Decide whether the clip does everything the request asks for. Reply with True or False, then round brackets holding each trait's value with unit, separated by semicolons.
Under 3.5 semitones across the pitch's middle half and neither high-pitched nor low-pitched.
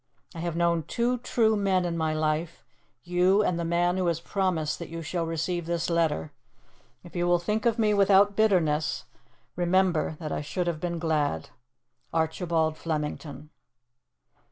True (2.7 semitones; 170 Hz)